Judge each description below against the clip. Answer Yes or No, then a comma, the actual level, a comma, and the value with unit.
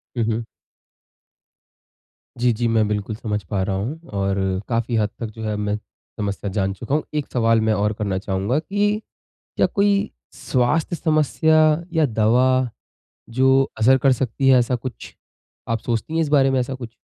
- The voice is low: Yes, low, 120 Hz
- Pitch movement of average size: Yes, average, 4.2 semitones